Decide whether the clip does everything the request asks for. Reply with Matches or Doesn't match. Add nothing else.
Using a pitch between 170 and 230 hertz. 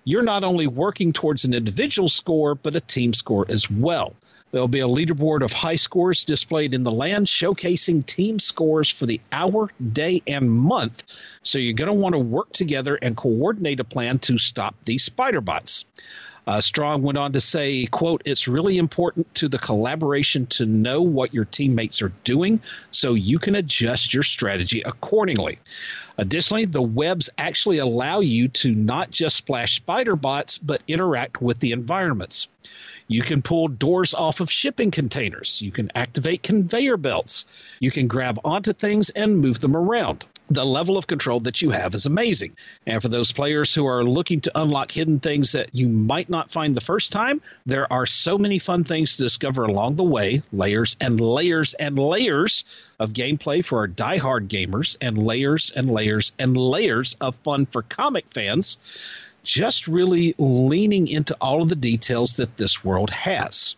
Doesn't match